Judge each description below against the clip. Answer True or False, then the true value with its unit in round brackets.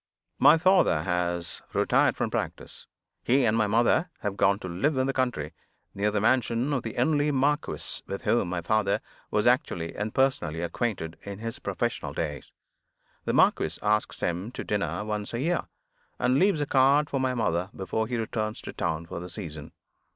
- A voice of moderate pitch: False (110 Hz)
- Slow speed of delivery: False (180 wpm)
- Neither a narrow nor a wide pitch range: False (6.4 semitones)